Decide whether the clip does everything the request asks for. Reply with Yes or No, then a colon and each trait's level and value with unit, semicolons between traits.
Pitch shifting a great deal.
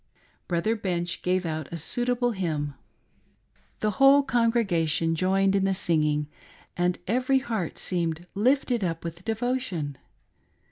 Yes: wide, 5.9 semitones